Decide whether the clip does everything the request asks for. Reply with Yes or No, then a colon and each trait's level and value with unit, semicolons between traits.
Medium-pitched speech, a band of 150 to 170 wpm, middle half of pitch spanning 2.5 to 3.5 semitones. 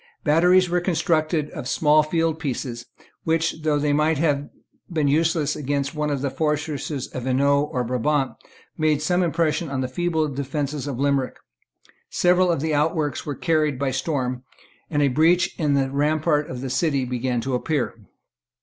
Yes: medium, 150 Hz; average, 160 wpm; average, 2.8 semitones